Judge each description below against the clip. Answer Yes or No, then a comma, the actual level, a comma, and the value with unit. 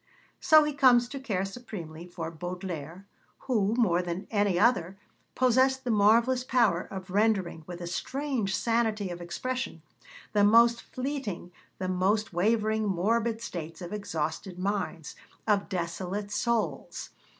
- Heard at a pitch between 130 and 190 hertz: No, high, 205 Hz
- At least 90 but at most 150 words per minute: Yes, slow, 135 wpm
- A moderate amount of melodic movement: Yes, average, 4.8 semitones